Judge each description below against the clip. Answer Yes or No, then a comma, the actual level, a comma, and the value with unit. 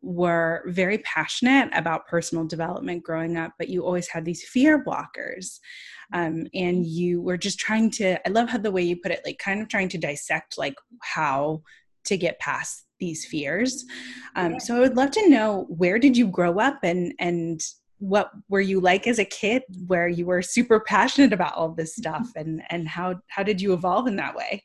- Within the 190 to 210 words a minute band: Yes, average, 200 wpm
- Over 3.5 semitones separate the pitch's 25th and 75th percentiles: Yes, average, 4.1 semitones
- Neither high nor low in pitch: Yes, medium, 180 Hz